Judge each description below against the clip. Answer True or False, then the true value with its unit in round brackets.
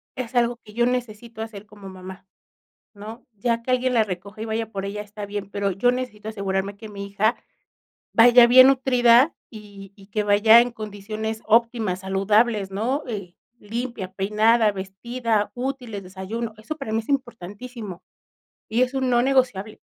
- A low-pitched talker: False (220 Hz)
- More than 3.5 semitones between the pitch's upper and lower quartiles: False (3.1 semitones)